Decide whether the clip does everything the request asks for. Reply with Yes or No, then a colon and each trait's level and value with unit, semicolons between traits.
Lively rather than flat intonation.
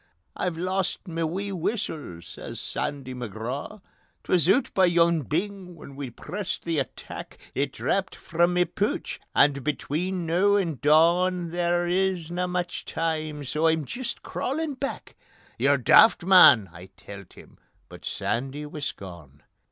No: average, 4.3 semitones